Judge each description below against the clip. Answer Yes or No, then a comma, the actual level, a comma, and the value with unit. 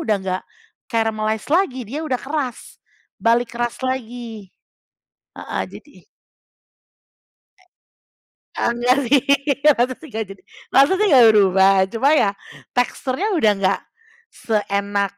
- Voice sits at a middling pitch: No, high, 235 Hz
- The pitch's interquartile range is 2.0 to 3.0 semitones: No, average, 4.1 semitones